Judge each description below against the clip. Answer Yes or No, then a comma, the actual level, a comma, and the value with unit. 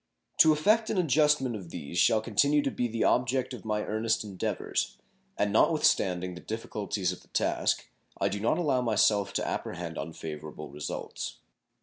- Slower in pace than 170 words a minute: No, average, 175 wpm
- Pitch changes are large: Yes, wide, 6.3 semitones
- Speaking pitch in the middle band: No, low, 110 Hz